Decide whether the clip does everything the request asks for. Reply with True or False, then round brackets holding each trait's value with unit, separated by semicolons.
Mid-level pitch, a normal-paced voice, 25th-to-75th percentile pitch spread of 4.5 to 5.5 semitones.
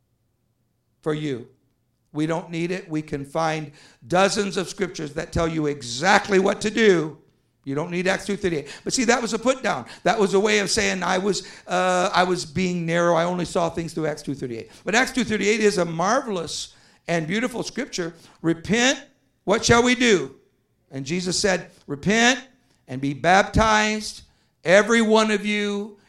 True (180 Hz; 190 wpm; 5.1 semitones)